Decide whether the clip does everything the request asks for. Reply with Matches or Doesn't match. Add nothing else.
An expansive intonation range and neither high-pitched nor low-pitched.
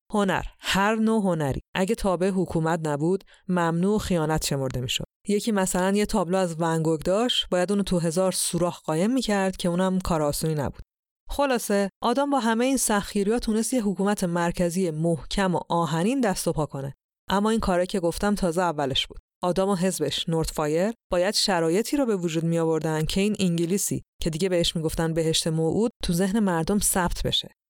Doesn't match